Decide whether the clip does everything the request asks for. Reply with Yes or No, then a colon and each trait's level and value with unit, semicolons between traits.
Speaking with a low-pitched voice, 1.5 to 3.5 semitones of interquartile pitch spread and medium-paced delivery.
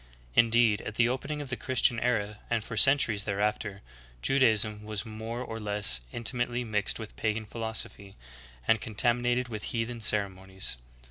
Yes: low, 110 Hz; narrow, 2.6 semitones; average, 160 wpm